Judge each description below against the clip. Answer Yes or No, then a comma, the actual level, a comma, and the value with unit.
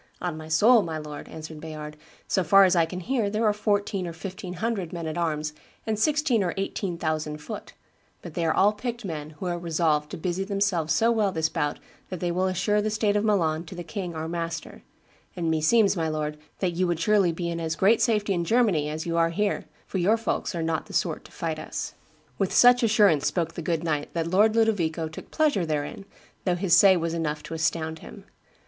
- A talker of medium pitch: Yes, medium, 175 Hz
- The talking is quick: Yes, fast, 225 wpm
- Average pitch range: Yes, average, 4.1 semitones